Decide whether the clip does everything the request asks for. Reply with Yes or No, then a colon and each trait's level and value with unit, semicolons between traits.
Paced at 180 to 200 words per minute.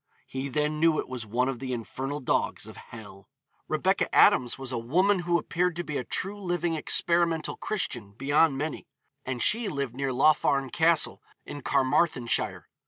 No: average, 170 wpm